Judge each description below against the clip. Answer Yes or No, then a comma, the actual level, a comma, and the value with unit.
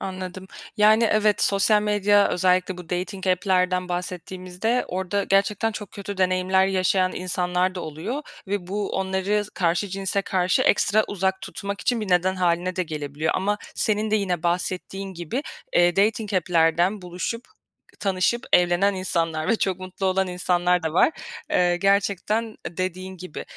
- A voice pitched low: No, medium, 185 Hz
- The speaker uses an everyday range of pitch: No, narrow, 2.1 semitones